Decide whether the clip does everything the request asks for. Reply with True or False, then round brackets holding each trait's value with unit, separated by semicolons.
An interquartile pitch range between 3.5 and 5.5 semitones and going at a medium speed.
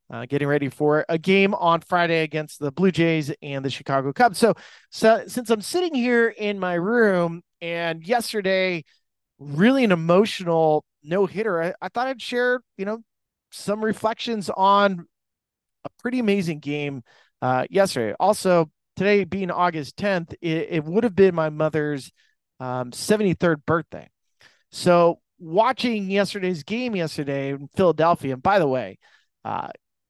True (5.1 semitones; 150 wpm)